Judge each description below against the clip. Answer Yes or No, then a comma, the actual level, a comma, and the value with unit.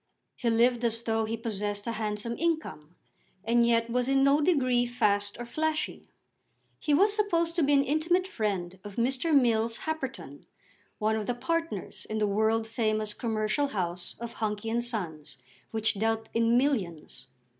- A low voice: No, high, 230 Hz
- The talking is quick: No, average, 165 wpm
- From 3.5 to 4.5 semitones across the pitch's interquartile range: Yes, average, 4.2 semitones